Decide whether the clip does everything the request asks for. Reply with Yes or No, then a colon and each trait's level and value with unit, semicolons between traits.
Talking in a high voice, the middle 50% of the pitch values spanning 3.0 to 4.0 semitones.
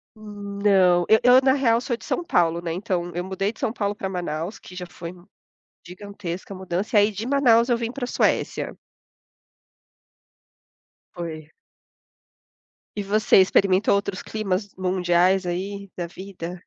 Yes: high, 195 Hz; average, 3.3 semitones